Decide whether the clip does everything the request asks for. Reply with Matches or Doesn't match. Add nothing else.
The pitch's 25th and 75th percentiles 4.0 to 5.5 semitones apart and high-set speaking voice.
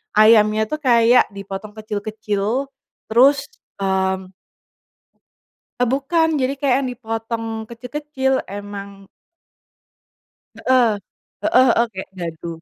Matches